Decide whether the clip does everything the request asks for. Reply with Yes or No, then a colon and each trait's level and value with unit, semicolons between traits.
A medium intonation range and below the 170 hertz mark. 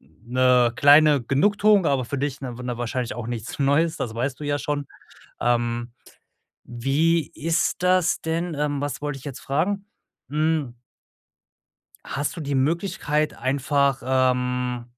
Yes: average, 3.6 semitones; medium, 140 Hz